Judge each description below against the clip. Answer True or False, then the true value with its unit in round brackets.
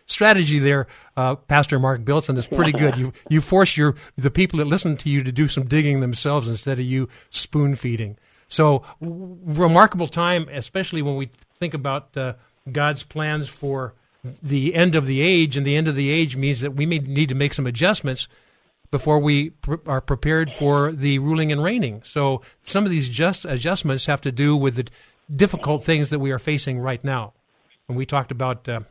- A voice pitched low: False (145 Hz)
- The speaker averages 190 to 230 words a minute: True (200 wpm)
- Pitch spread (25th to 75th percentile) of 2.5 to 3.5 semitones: True (2.9 semitones)